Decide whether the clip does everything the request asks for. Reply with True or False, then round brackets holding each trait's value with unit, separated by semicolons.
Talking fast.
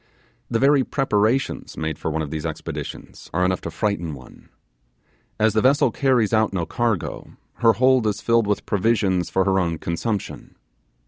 False (170 wpm)